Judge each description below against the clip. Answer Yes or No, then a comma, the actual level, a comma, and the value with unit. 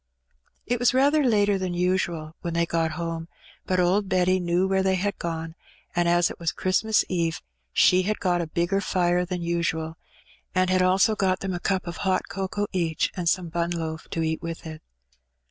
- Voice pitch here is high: No, medium, 180 Hz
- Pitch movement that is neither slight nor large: No, narrow, 2.2 semitones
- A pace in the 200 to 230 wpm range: Yes, fast, 205 wpm